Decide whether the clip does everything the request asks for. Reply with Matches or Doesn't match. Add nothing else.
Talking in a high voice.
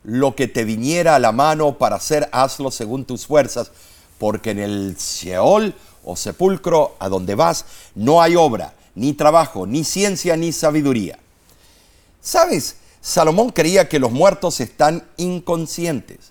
Doesn't match